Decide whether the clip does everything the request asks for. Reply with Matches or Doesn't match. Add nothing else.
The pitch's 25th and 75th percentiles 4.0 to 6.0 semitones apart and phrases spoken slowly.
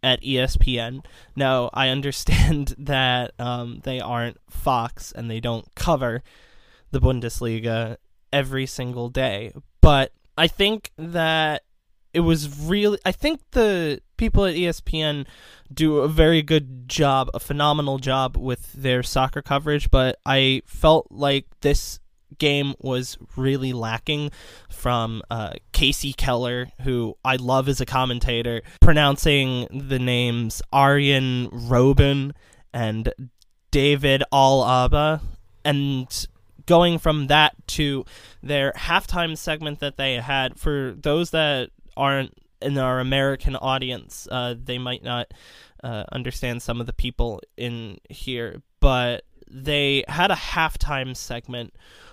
Doesn't match